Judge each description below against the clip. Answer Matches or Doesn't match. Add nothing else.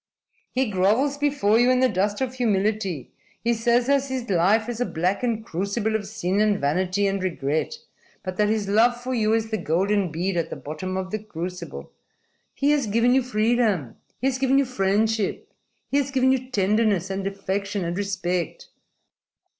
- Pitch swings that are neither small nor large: Matches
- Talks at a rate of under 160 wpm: Doesn't match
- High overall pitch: Matches